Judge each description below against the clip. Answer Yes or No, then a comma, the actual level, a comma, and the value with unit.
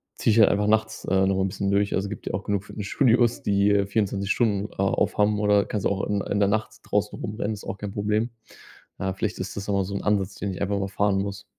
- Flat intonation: Yes, narrow, 1.1 semitones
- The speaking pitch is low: Yes, low, 100 Hz